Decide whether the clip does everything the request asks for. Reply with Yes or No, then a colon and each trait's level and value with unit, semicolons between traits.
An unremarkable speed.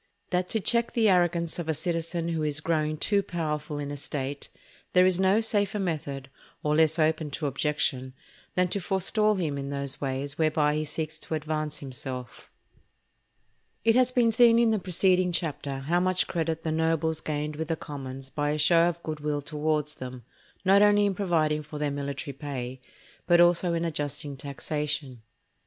Yes: average, 180 wpm